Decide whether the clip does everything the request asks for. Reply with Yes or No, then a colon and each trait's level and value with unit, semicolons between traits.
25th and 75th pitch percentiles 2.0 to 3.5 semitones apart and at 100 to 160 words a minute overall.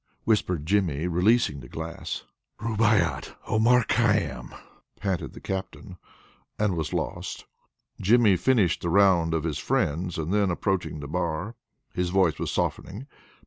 No: average, 4.0 semitones; slow, 135 wpm